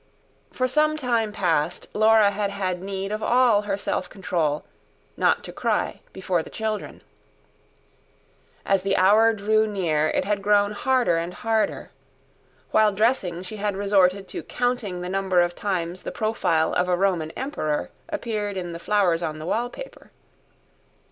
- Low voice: No, high, 200 Hz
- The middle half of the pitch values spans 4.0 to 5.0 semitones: No, average, 3.4 semitones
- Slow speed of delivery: No, average, 155 wpm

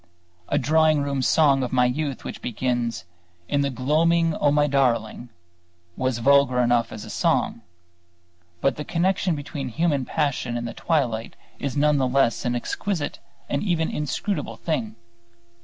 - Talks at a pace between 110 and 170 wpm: Yes, average, 155 wpm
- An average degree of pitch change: Yes, average, 3.7 semitones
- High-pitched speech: No, medium, 140 Hz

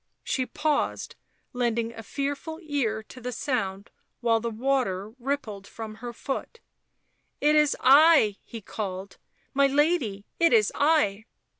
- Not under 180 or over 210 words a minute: No, average, 145 wpm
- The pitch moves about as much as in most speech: Yes, average, 4.8 semitones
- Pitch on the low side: No, high, 245 Hz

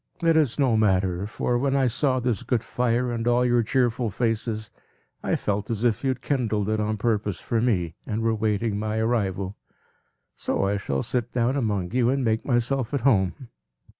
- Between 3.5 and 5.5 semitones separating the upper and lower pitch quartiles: No, average, 2.9 semitones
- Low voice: Yes, low, 115 Hz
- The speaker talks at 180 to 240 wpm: Yes, average, 195 wpm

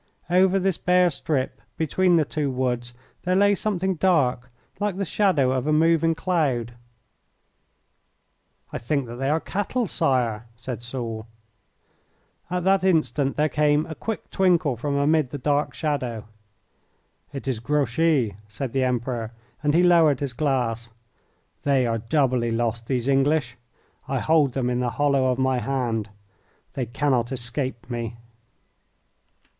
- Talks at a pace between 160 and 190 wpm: No, average, 145 wpm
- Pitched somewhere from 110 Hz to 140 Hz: Yes, low, 135 Hz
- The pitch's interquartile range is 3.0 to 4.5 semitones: No, average, 4.9 semitones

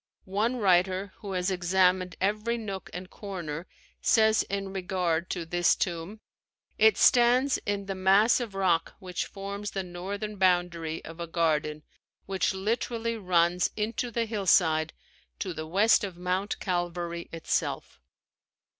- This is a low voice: No, high, 190 Hz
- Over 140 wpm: No, slow, 135 wpm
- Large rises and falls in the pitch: No, average, 2.9 semitones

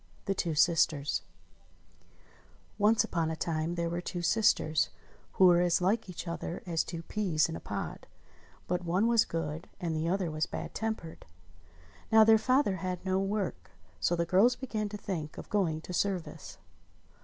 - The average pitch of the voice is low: No, medium, 175 Hz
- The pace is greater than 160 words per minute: Yes, average, 170 wpm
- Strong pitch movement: No, average, 3.7 semitones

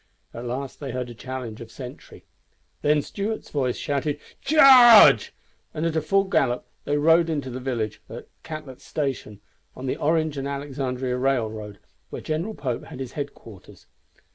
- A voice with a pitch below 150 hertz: Yes, low, 135 Hz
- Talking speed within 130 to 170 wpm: Yes, average, 155 wpm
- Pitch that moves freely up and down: No, average, 3.8 semitones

